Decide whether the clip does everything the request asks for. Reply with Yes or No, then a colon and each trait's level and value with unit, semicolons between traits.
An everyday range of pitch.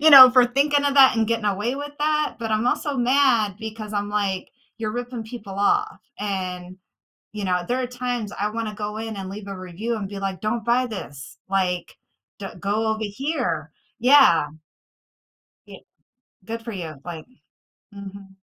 Yes: average, 4.0 semitones